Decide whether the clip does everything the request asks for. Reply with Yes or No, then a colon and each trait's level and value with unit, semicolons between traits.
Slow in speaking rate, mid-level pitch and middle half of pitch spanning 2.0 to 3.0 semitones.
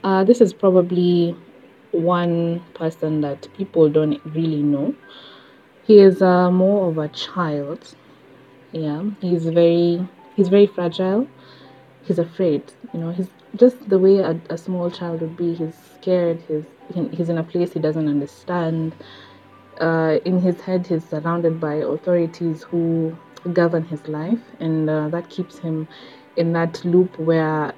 No: average, 150 wpm; medium, 170 Hz; narrow, 2.5 semitones